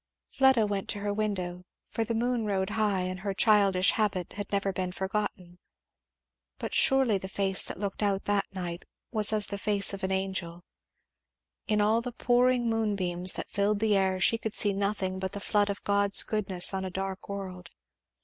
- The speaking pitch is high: Yes, high, 200 Hz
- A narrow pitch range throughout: Yes, narrow, 2.0 semitones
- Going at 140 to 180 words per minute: No, average, 190 wpm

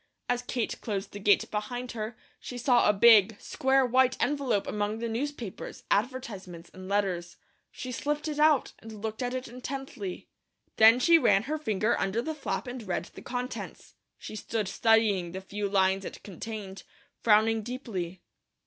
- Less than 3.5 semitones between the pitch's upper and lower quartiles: No, average, 3.9 semitones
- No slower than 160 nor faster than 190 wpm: Yes, average, 165 wpm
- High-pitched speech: Yes, high, 225 Hz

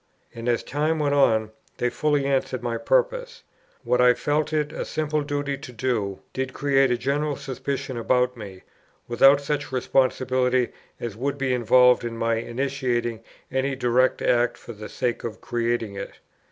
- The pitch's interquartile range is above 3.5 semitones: No, average, 3.0 semitones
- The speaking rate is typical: Yes, average, 165 wpm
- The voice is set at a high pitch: No, low, 130 Hz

